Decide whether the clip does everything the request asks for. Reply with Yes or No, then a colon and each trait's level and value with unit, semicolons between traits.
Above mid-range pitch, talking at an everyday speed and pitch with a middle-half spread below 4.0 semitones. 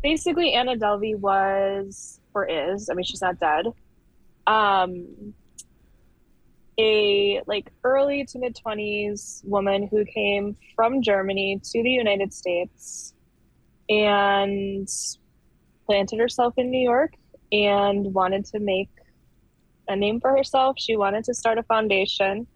No: high, 210 Hz; slow, 125 wpm; average, 3.6 semitones